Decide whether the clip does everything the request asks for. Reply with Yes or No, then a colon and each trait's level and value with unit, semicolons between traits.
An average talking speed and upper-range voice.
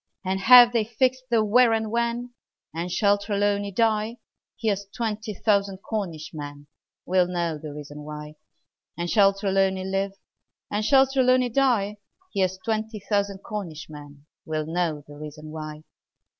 Yes: average, 145 wpm; high, 200 Hz